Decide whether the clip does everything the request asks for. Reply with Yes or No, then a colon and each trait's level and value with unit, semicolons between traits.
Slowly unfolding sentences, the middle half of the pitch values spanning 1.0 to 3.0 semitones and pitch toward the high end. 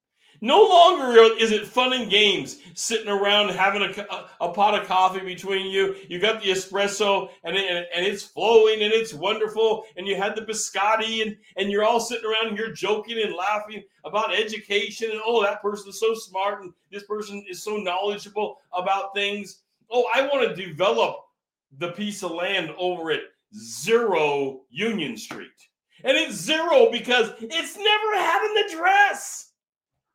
No: average, 170 wpm; narrow, 2.6 semitones; high, 205 Hz